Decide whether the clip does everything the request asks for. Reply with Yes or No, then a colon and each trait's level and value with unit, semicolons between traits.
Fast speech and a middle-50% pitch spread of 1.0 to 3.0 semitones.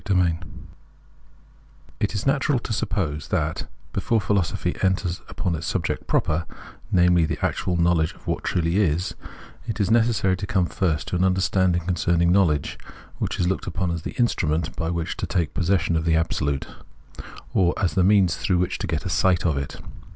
No: average, 185 wpm; narrow, 2.6 semitones